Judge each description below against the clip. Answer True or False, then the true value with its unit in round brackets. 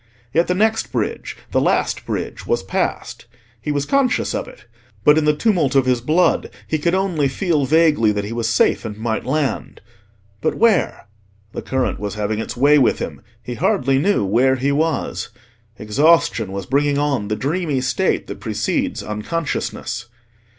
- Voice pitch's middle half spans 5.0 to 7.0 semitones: True (5.5 semitones)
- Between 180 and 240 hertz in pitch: False (140 Hz)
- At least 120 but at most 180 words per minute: True (165 wpm)